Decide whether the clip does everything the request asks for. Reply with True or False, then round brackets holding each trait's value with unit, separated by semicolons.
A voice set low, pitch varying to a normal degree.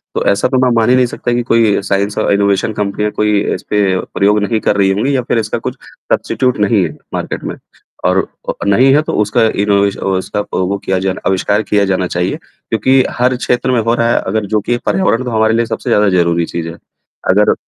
True (105 Hz; 3.0 semitones)